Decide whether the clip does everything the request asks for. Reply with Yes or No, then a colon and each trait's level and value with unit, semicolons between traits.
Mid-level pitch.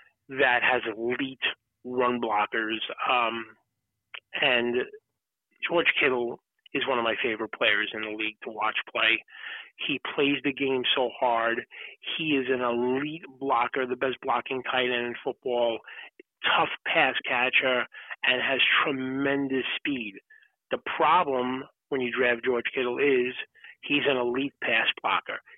No: low, 130 Hz